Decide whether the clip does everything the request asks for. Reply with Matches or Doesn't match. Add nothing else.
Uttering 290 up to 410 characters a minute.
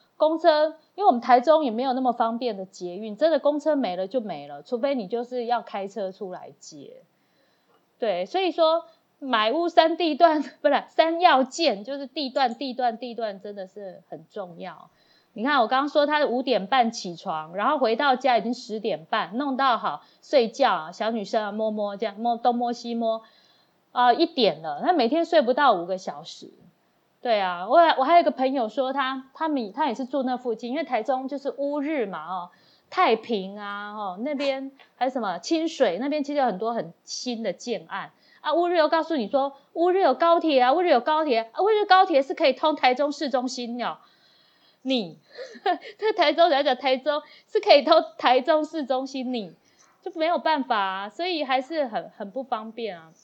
Doesn't match